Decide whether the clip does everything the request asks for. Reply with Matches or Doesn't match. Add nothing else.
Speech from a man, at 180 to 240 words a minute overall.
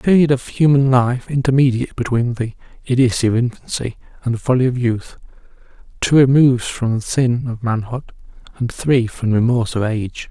Doesn't match